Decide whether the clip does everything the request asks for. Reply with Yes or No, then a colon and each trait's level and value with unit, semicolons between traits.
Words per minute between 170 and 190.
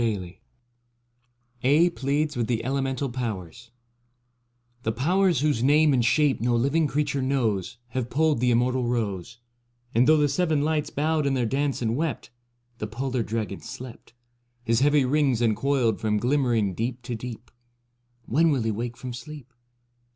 No: average, 155 wpm